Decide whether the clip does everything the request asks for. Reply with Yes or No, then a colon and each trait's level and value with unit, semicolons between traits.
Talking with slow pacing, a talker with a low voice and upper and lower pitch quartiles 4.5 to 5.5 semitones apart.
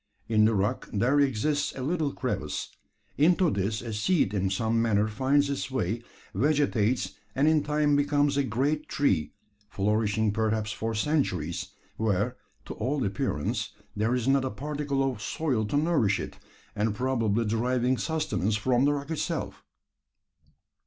No: average, 150 wpm; low, 125 Hz; average, 5.1 semitones